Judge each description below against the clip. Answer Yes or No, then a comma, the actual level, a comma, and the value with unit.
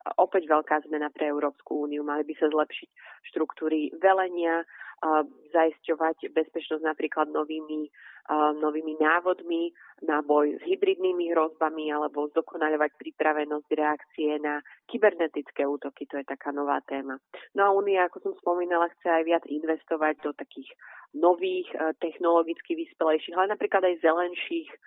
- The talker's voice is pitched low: No, medium, 160 Hz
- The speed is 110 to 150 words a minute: Yes, average, 130 wpm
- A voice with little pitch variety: No, average, 3.2 semitones